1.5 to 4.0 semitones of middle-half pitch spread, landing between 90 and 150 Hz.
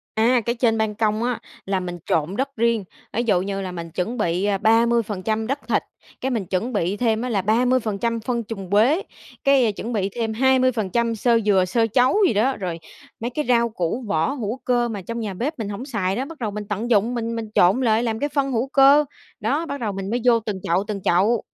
No: average, 3.5 semitones; high, 225 Hz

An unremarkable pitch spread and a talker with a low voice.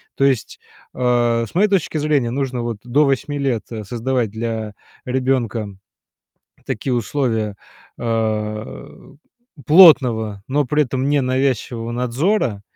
Yes: average, 3.5 semitones; low, 125 Hz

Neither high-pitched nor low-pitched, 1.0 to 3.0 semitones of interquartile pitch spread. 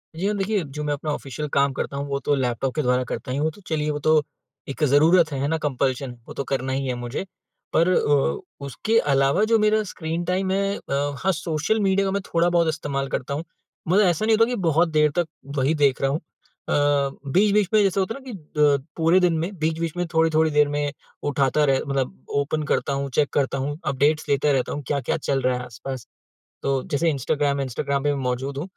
No: medium, 145 Hz; average, 3.5 semitones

